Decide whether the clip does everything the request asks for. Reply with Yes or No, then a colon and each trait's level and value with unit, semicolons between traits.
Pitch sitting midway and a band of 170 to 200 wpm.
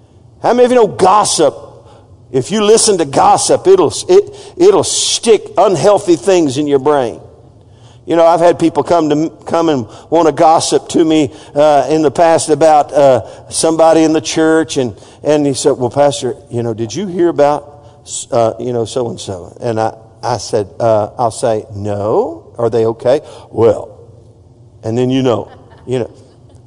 Yes: medium, 145 Hz; average, 190 wpm